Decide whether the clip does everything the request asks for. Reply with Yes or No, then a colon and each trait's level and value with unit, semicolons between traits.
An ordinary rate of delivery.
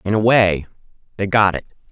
Yes: average, 190 wpm